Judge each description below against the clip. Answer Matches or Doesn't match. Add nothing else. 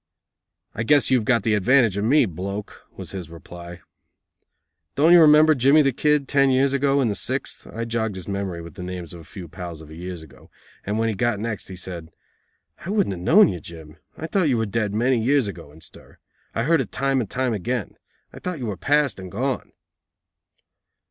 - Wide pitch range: Matches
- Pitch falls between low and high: Doesn't match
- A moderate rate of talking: Doesn't match